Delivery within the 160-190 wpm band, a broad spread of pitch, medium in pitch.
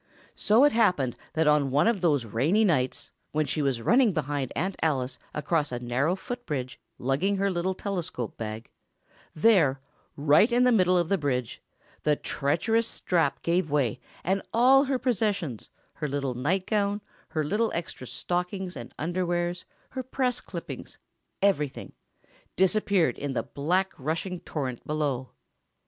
No: average, 140 wpm; wide, 6.0 semitones; medium, 170 Hz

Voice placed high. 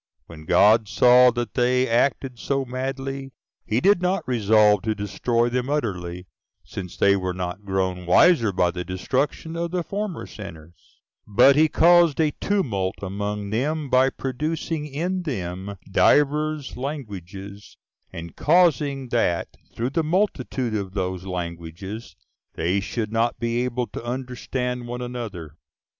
No: low, 120 Hz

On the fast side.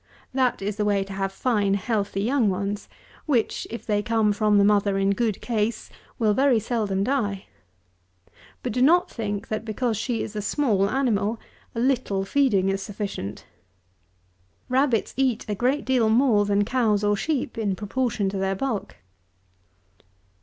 No: average, 160 wpm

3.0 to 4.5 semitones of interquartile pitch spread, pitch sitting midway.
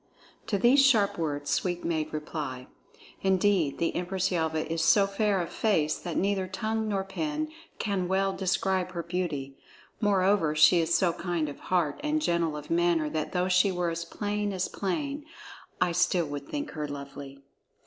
Yes: average, 3.7 semitones; medium, 180 Hz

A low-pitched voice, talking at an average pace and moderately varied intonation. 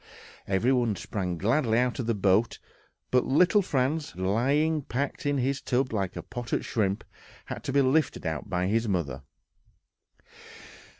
No: low, 120 Hz; average, 155 wpm; wide, 5.9 semitones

